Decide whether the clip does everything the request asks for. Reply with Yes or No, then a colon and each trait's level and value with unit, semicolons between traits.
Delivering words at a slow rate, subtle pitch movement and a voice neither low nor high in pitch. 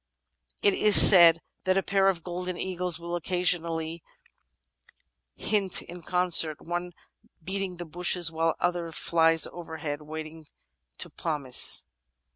Yes: slow, 125 wpm; narrow, 1.9 semitones; medium, 175 Hz